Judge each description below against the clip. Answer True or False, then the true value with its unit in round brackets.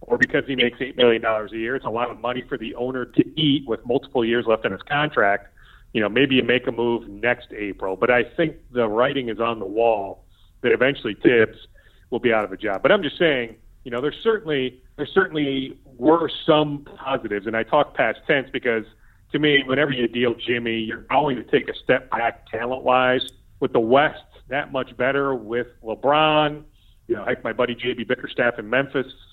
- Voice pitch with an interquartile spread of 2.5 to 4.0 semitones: True (3.0 semitones)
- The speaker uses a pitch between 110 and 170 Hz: True (120 Hz)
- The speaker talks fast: True (210 wpm)